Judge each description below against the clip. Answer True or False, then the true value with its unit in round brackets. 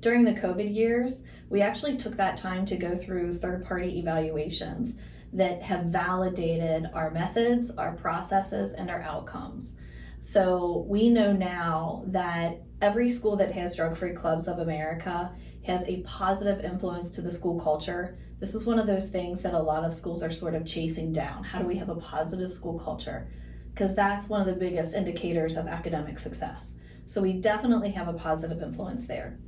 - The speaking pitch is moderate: True (180 Hz)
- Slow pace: False (180 wpm)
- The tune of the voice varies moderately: True (3.2 semitones)